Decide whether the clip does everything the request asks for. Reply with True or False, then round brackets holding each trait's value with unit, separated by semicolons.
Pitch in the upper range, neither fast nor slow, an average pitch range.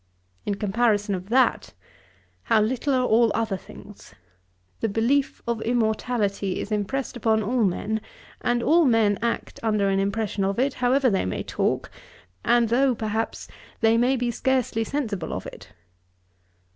True (225 Hz; 150 wpm; 3.1 semitones)